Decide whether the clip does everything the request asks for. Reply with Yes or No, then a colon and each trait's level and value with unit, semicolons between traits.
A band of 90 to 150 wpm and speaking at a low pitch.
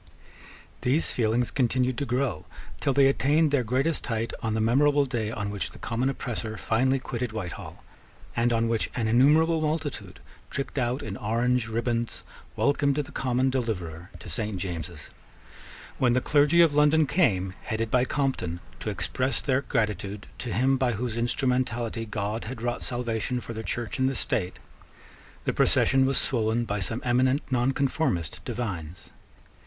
No: average, 160 wpm; low, 120 Hz